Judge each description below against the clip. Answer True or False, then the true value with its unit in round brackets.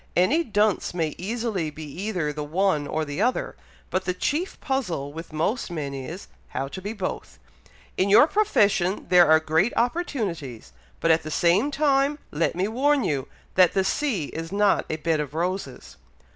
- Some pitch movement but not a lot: False (6.1 semitones)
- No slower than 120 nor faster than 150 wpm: False (175 wpm)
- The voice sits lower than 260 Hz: True (185 Hz)